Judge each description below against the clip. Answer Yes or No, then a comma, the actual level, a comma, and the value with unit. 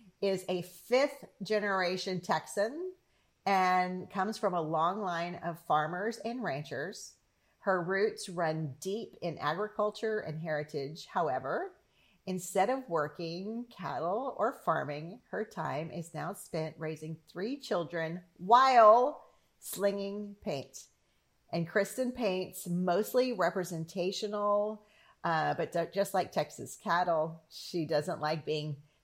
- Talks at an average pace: No, slow, 120 wpm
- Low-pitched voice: No, medium, 185 Hz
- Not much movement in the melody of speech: No, average, 4.3 semitones